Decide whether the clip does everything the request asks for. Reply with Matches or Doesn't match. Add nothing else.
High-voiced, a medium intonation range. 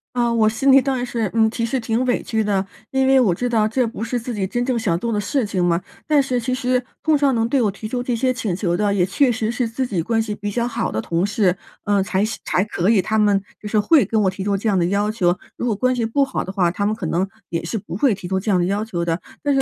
Matches